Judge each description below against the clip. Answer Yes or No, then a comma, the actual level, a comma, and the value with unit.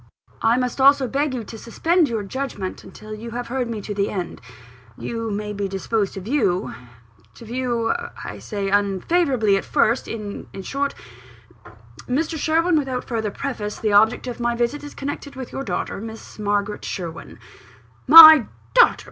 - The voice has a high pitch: Yes, high, 230 Hz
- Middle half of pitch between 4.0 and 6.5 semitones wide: Yes, average, 4.8 semitones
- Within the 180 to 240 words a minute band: No, average, 170 wpm